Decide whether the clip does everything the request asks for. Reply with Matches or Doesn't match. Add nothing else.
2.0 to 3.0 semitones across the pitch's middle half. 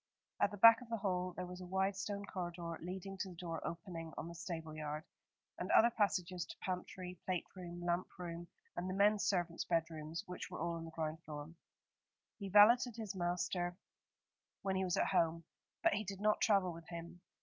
Matches